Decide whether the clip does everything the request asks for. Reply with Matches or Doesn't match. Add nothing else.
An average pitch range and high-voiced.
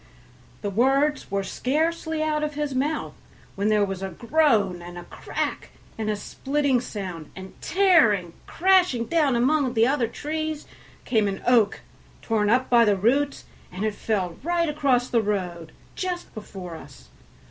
Doesn't match